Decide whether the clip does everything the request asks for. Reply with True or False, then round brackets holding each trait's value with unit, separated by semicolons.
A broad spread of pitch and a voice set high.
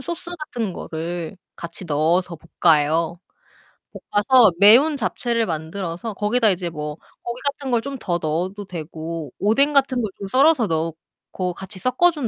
True (6.8 semitones; 195 Hz)